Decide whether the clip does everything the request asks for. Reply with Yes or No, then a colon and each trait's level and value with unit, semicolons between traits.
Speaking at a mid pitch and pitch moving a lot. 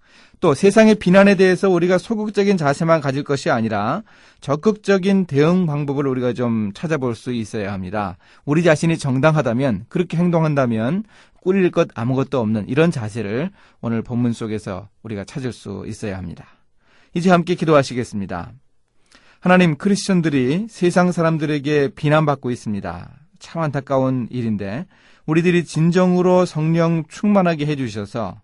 Yes: medium, 145 Hz; wide, 7.3 semitones